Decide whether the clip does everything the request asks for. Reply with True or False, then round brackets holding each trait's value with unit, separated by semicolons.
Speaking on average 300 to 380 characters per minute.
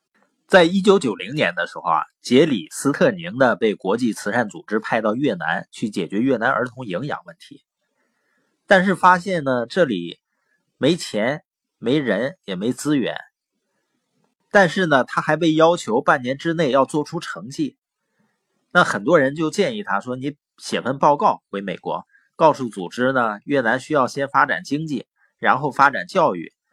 False (240 characters per minute)